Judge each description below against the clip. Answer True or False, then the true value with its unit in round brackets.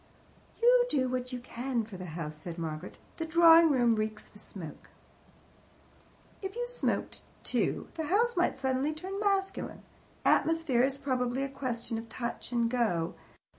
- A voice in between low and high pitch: False (255 Hz)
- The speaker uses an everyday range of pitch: False (6.4 semitones)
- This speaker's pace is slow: False (155 wpm)